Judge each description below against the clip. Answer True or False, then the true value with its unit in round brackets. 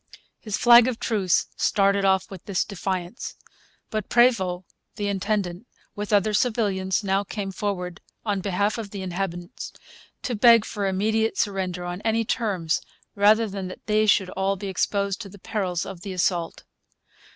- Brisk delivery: False (155 wpm)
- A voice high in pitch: True (200 Hz)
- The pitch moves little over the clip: True (2.3 semitones)